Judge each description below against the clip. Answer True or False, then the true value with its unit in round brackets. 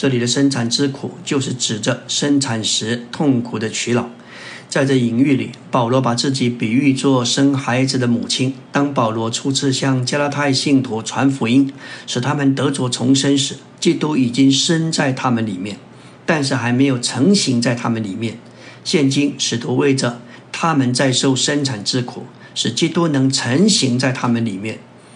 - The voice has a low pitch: True (130 Hz)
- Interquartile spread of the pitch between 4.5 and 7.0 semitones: False (2.5 semitones)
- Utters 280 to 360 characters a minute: False (255 characters per minute)